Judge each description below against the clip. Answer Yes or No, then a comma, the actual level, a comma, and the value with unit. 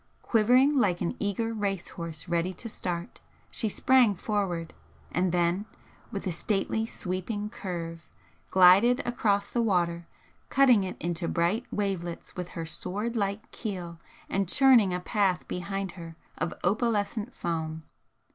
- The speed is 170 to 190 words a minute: No, slow, 135 wpm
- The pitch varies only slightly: No, average, 3.8 semitones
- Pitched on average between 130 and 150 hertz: No, high, 195 Hz